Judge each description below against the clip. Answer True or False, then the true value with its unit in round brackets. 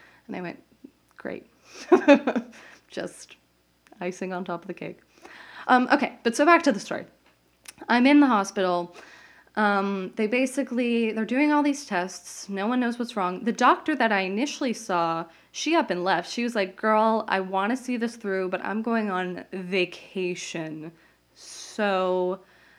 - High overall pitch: True (215 Hz)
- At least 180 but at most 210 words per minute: False (165 wpm)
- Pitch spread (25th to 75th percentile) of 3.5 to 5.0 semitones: False (5.4 semitones)